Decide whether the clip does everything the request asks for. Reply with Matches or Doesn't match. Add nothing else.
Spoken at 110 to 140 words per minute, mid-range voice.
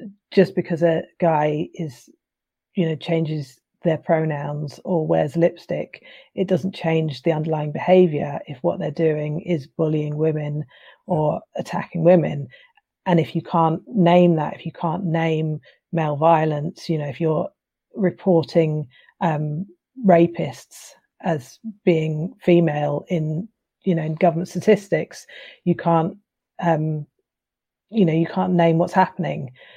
Matches